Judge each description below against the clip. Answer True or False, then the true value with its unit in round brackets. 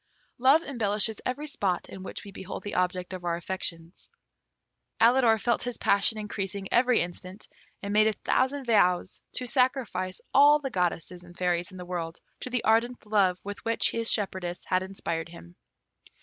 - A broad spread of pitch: False (4.8 semitones)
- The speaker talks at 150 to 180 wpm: True (170 wpm)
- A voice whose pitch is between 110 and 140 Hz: False (200 Hz)